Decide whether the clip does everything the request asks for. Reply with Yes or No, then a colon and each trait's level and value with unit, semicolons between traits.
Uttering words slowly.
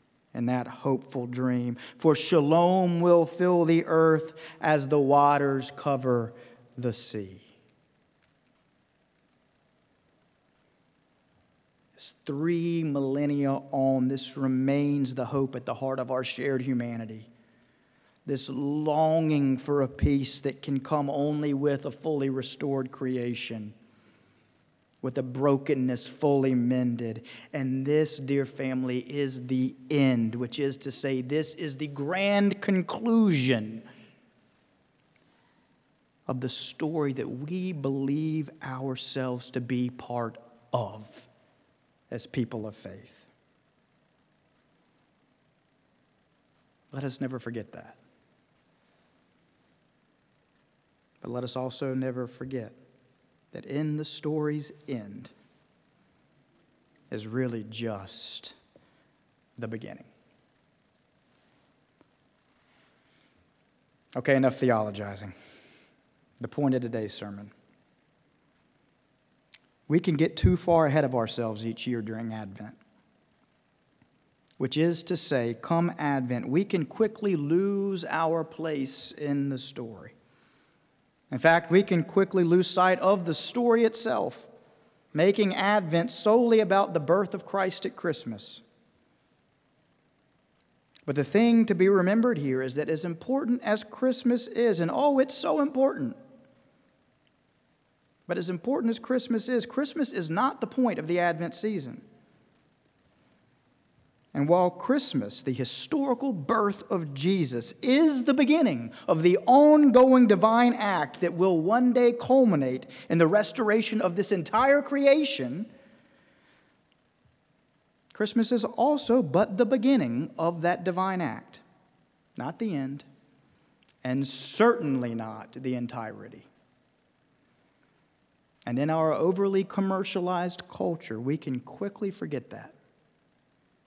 Yes: slow, 110 wpm